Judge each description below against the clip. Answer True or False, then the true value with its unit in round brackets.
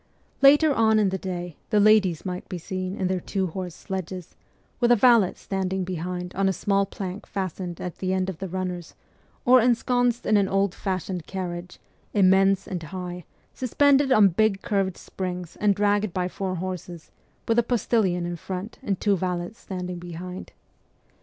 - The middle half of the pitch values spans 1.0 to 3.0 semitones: True (2.4 semitones)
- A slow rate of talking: False (170 wpm)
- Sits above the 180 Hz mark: True (190 Hz)